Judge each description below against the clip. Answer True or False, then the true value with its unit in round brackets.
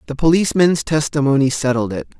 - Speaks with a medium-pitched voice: True (145 Hz)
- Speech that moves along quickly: False (135 wpm)